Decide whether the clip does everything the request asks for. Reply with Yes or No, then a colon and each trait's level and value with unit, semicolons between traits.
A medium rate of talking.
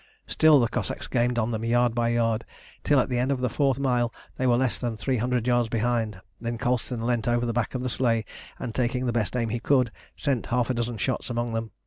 No: fast, 245 wpm